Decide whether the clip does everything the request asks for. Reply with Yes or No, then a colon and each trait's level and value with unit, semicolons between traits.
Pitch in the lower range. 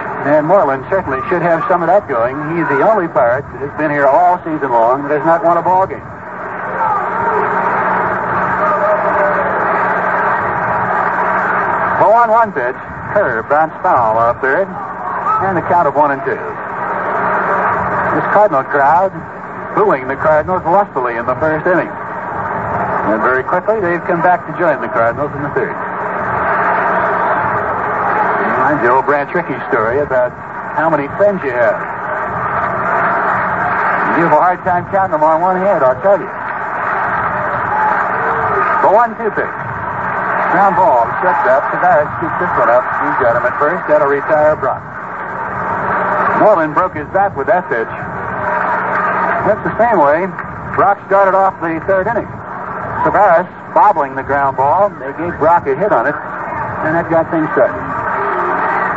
No: high, 190 Hz